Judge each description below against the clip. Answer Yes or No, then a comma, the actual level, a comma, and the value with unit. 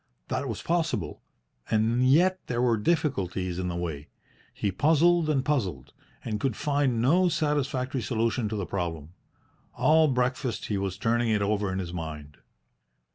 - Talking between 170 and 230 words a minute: No, average, 155 wpm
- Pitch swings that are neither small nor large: No, wide, 7.0 semitones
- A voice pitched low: Yes, low, 115 Hz